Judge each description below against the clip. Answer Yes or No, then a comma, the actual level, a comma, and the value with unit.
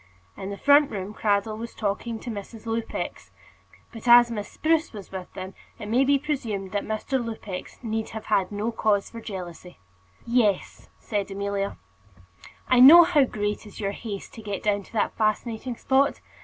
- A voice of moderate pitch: No, high, 220 Hz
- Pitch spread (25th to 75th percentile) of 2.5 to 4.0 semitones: Yes, average, 2.9 semitones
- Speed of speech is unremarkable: Yes, average, 175 wpm